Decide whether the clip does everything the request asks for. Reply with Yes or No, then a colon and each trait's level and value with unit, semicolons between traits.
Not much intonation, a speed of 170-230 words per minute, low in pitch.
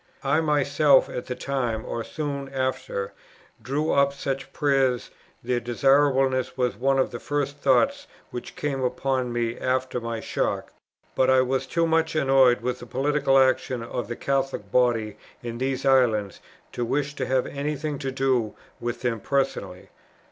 No: narrow, 2.3 semitones; average, 160 wpm; low, 130 Hz